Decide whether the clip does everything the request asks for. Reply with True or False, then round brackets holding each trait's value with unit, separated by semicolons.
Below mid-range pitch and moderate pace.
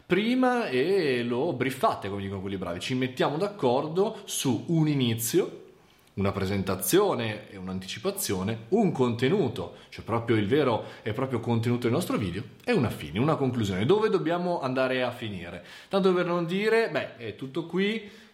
True (130 Hz; 155 wpm)